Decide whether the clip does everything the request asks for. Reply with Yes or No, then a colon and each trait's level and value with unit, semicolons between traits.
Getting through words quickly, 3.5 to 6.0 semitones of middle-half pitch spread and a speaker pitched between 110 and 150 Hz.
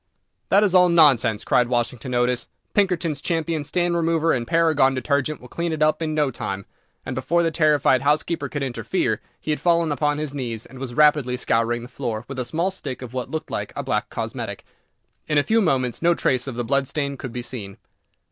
Yes: fast, 210 wpm; average, 4.6 semitones; medium, 140 Hz